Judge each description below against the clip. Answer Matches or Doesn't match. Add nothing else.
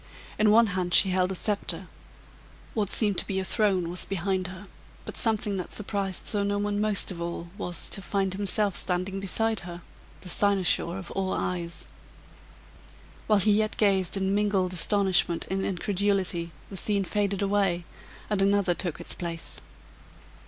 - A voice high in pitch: Matches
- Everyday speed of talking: Matches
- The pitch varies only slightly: Matches